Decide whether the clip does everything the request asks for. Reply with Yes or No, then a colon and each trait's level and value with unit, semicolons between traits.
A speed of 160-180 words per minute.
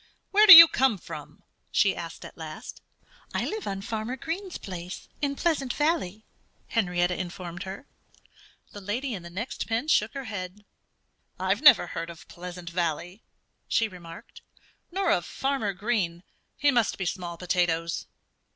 No: average, 150 wpm